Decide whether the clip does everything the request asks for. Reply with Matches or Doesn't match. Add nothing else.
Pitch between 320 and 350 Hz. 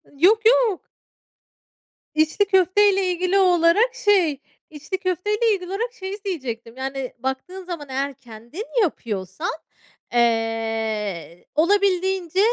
Matches